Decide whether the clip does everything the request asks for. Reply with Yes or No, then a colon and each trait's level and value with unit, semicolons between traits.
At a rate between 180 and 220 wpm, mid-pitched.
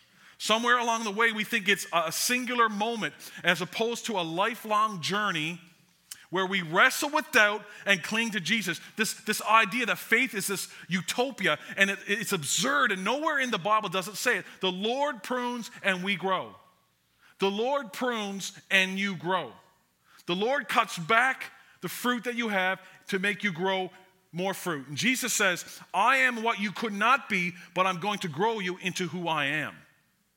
No: average, 185 wpm; high, 200 Hz